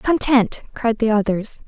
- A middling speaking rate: Yes, average, 145 wpm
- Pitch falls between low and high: No, high, 230 Hz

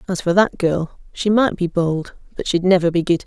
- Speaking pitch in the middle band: Yes, medium, 180 Hz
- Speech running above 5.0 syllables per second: Yes, 5.5 syllables/s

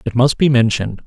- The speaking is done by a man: Yes, male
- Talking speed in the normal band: No, fast, 225 wpm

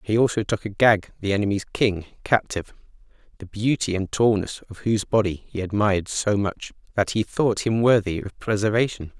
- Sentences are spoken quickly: No, average, 165 wpm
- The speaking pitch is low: Yes, low, 105 Hz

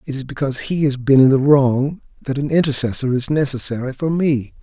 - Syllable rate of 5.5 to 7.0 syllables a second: Yes, 5.6 syllables/s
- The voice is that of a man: Yes, male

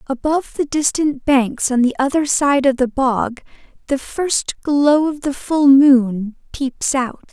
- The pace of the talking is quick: No, average, 165 wpm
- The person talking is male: No, female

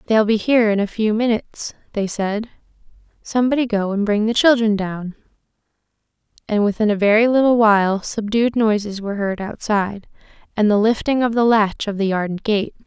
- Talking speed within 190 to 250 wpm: No, average, 175 wpm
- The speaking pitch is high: Yes, high, 215 Hz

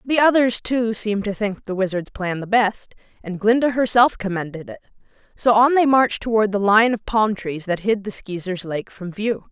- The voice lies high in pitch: Yes, high, 210 Hz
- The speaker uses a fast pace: Yes, fast, 210 wpm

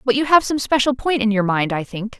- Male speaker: No, female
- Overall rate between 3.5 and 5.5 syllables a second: No, 5.7 syllables/s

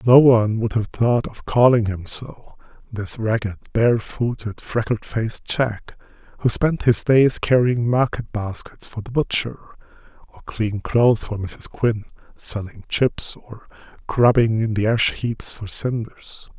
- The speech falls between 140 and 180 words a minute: Yes, average, 150 wpm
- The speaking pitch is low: Yes, low, 115 Hz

